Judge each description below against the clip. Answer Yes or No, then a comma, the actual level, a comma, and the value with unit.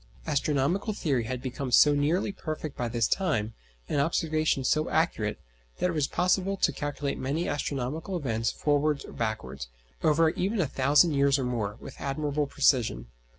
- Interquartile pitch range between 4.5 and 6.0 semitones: No, average, 3.9 semitones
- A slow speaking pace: No, average, 160 wpm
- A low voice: No, medium, 145 Hz